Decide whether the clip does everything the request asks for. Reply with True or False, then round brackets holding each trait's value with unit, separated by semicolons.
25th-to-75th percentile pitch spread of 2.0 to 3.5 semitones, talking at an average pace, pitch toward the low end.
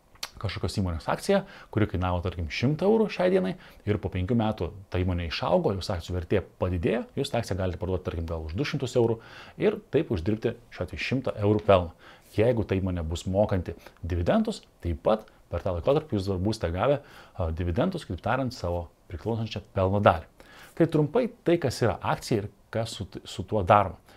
False (5.0 semitones; 175 wpm; 105 Hz)